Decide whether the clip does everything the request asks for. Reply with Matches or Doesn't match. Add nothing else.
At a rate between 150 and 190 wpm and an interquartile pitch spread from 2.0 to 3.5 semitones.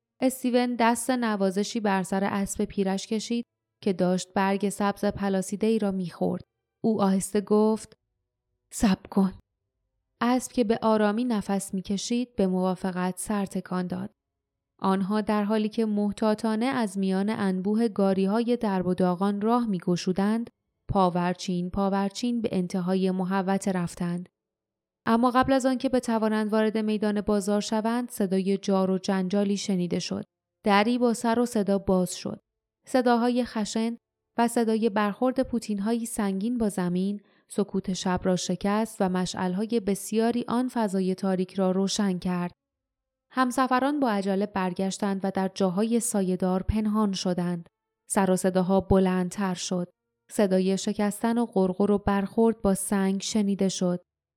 Doesn't match